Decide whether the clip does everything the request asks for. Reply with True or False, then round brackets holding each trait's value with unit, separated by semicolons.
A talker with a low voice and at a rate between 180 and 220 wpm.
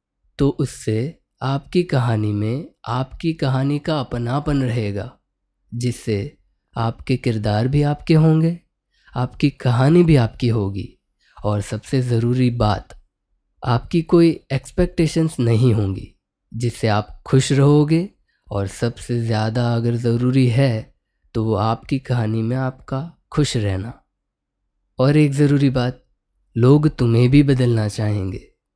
False (125 Hz; 120 wpm)